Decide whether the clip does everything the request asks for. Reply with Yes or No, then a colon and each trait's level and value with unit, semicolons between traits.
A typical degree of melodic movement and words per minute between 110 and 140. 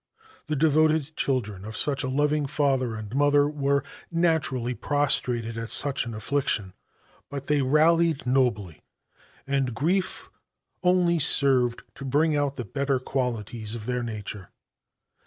Yes: average, 3.8 semitones; slow, 135 wpm